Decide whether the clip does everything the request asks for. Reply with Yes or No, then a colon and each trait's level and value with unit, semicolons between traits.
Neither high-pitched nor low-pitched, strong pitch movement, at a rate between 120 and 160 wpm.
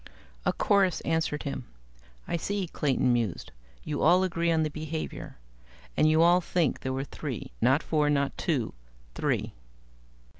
No: medium, 155 Hz; average, 3.3 semitones; average, 150 wpm